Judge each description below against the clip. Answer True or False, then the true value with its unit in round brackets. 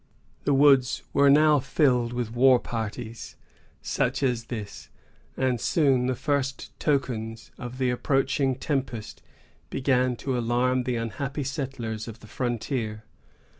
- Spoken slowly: True (130 wpm)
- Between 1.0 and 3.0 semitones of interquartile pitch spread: True (2.6 semitones)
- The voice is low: True (125 Hz)